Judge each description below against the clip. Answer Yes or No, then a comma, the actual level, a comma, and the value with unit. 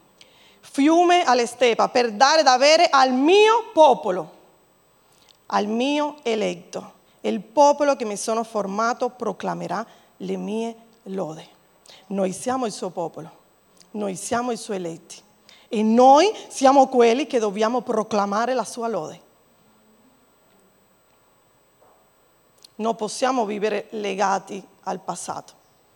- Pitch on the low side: No, high, 230 Hz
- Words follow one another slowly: Yes, slow, 110 wpm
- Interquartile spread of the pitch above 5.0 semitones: No, average, 3.9 semitones